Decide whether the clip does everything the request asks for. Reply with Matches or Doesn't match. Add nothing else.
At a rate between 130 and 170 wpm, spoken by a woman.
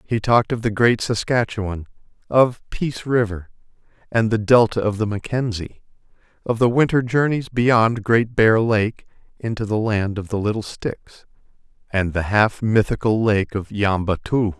Doesn't match